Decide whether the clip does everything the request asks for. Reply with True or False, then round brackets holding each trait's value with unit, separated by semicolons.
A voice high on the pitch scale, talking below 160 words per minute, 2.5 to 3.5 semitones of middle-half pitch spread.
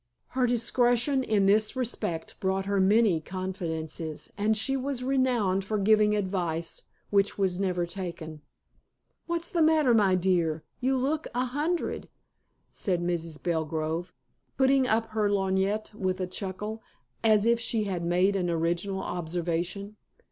False (195 Hz; 140 wpm; 4.7 semitones)